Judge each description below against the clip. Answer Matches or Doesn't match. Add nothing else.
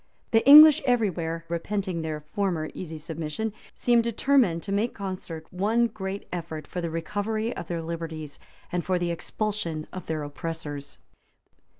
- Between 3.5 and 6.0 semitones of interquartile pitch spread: Matches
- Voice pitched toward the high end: Doesn't match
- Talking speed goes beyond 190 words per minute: Doesn't match